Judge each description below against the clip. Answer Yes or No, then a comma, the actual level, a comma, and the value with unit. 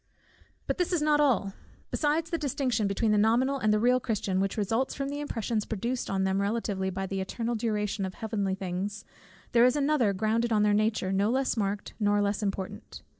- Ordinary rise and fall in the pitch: Yes, average, 4.1 semitones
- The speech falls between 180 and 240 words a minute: Yes, average, 200 wpm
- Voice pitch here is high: Yes, high, 215 Hz